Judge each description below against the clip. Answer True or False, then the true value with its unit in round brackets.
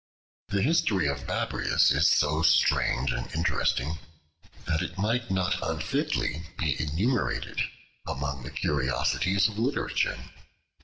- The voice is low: True (80 Hz)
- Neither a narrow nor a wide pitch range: False (5.9 semitones)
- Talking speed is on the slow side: True (115 wpm)